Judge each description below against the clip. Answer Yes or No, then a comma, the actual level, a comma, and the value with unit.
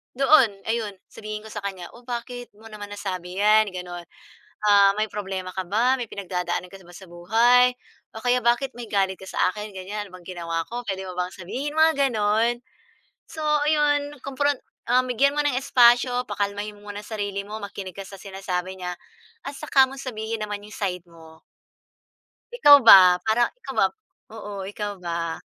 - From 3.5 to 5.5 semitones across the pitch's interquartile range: Yes, average, 4.4 semitones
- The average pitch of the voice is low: No, high, 210 Hz